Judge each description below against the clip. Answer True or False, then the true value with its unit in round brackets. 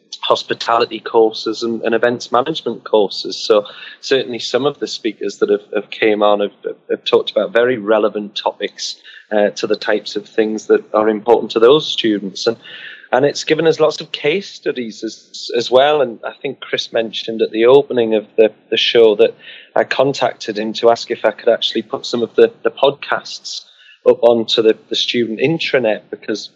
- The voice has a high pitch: False (125 Hz)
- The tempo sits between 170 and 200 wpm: True (190 wpm)